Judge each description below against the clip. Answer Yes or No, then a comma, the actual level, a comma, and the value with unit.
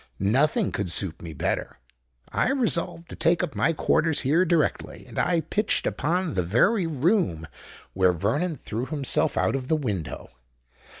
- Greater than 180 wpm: No, average, 155 wpm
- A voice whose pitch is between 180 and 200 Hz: No, medium, 150 Hz